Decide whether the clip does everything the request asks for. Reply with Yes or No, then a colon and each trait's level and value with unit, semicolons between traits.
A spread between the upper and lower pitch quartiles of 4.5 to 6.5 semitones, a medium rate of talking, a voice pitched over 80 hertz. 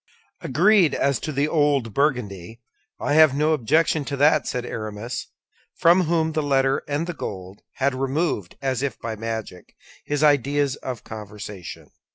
Yes: average, 5.1 semitones; average, 150 wpm; low, 135 Hz